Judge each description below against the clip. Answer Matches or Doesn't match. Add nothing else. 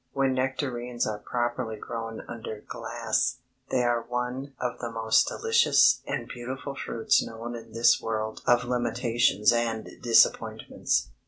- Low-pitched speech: Matches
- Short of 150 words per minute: Matches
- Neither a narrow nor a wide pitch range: Doesn't match